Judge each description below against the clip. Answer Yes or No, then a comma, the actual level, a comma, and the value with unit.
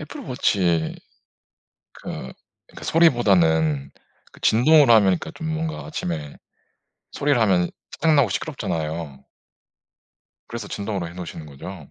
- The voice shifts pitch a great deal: Yes, wide, 8.0 semitones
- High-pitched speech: No, very low, 95 Hz